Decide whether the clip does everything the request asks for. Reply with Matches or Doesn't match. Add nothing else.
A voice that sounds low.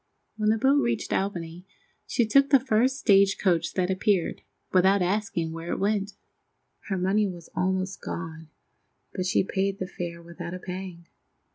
Doesn't match